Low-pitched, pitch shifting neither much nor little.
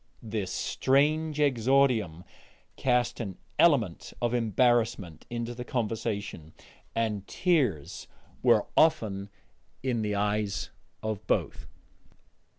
Yes: low, 115 Hz; average, 4.1 semitones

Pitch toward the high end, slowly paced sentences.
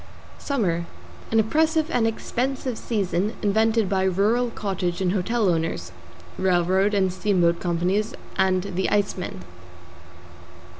Yes: high, 195 Hz; slow, 110 wpm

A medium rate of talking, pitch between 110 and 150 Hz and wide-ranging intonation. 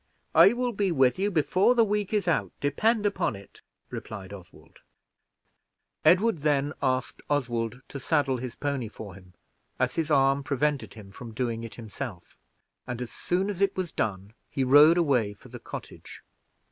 Yes: average, 170 wpm; medium, 140 Hz; wide, 7.3 semitones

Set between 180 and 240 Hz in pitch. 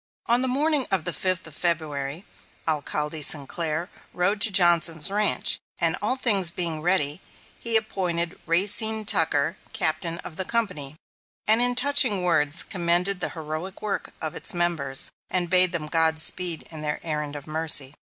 No: medium, 170 Hz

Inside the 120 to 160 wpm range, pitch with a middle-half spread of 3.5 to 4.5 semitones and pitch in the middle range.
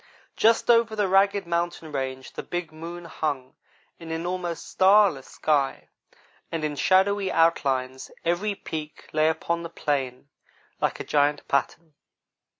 Yes: average, 140 wpm; average, 4.1 semitones; medium, 165 Hz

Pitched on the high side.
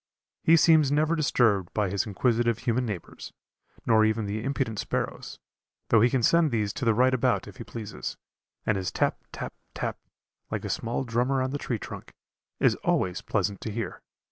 No: low, 115 Hz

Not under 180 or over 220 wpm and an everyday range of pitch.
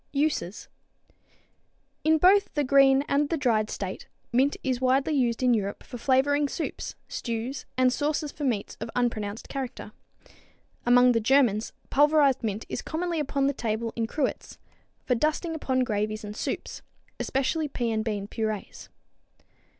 No: average, 150 wpm; average, 4.2 semitones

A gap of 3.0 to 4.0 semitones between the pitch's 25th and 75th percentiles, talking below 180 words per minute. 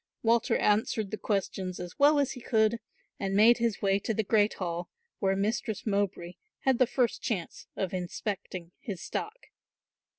Yes: average, 3.4 semitones; average, 165 wpm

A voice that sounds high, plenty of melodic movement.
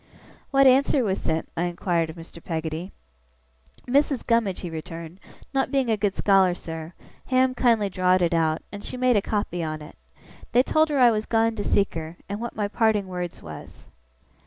Yes: high, 200 Hz; wide, 6.0 semitones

